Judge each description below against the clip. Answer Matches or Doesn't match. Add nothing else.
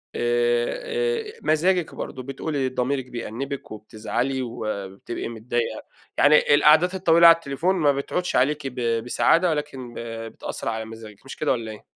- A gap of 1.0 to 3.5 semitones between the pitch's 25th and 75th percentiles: Doesn't match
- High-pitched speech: Doesn't match